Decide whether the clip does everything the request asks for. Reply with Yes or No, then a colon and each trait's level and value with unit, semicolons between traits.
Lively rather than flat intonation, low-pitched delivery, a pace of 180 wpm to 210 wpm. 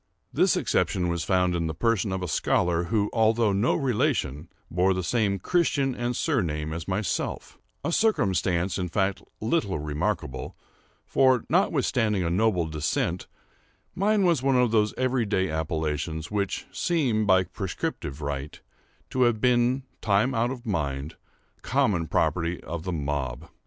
No: wide, 6.5 semitones; very low, 95 Hz; average, 145 wpm